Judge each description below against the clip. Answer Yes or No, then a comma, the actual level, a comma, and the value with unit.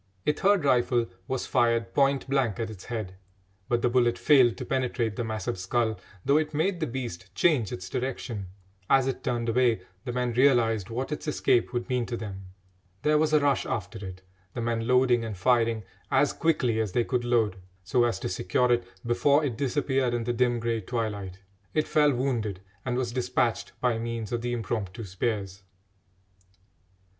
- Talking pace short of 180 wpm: No, average, 185 wpm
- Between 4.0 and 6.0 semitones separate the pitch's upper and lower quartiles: No, average, 2.7 semitones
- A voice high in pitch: No, low, 120 Hz